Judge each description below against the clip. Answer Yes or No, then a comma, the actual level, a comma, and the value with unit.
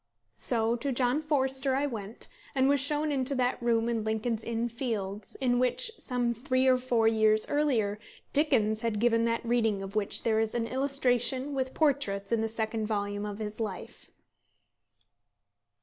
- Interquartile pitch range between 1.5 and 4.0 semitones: Yes, average, 3.2 semitones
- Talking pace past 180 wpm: No, average, 165 wpm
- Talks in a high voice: Yes, high, 235 Hz